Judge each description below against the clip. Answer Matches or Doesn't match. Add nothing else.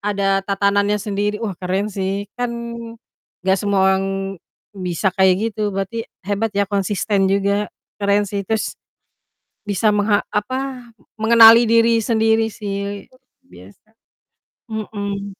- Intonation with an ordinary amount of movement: Doesn't match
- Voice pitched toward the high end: Matches